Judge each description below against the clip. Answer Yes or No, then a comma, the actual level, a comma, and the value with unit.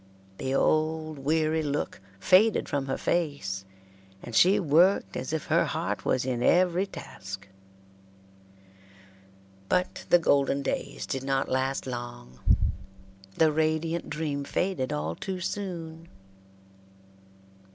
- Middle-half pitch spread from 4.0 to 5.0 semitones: Yes, average, 4.4 semitones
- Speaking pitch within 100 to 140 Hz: No, medium, 150 Hz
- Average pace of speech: No, slow, 115 wpm